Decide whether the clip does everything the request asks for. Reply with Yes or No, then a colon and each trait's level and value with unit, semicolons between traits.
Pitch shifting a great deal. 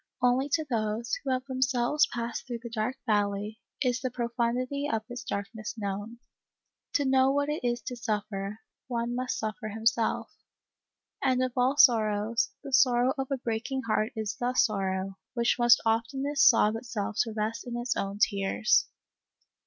No: average, 2.9 semitones